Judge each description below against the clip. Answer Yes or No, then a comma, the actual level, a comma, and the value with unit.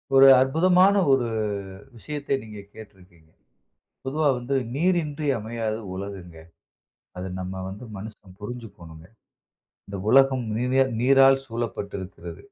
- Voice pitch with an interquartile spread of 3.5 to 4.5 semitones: No, wide, 5.6 semitones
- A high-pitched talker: No, low, 115 Hz